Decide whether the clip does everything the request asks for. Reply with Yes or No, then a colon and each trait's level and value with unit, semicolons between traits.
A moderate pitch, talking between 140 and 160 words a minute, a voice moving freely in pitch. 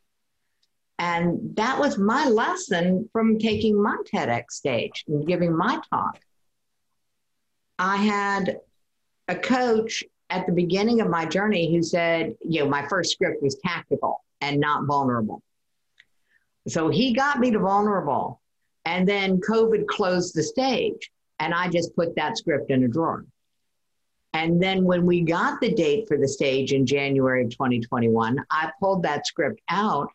Yes: medium, 175 Hz; average, 150 wpm; wide, 6.0 semitones